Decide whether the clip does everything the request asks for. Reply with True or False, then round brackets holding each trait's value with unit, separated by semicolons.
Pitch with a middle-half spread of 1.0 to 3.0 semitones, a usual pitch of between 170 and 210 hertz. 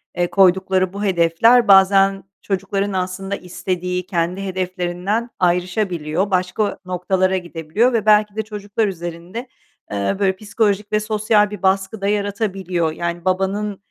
True (2.4 semitones; 190 Hz)